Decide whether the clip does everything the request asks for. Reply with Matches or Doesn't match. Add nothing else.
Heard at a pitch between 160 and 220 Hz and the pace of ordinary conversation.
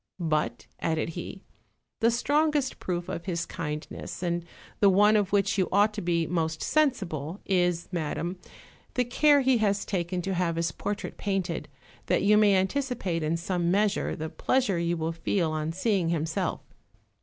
Matches